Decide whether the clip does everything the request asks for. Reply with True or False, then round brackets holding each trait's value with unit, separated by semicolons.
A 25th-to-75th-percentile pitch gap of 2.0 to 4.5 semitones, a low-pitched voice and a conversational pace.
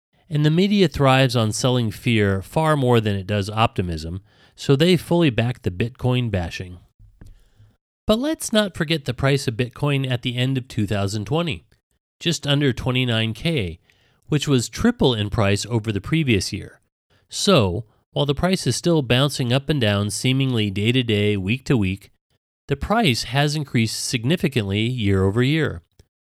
False (5.5 semitones; 125 Hz; 160 wpm)